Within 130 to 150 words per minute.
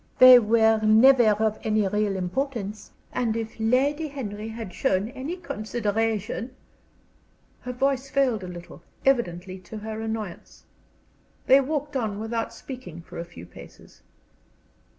Yes: average, 140 wpm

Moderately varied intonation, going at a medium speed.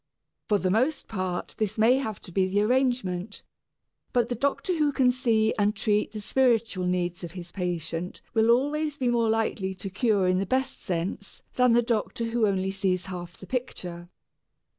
Yes: average, 4.6 semitones; average, 185 wpm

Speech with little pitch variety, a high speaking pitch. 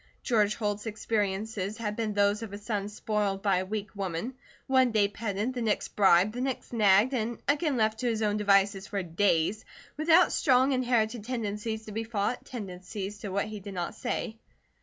Yes: narrow, 2.2 semitones; high, 210 Hz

